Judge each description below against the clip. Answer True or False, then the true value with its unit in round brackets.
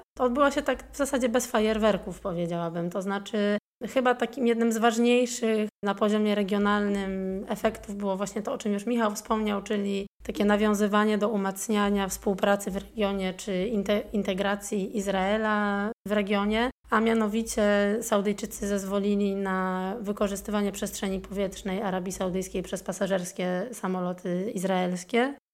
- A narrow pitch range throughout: True (2.0 semitones)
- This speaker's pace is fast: False (130 wpm)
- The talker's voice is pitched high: True (205 Hz)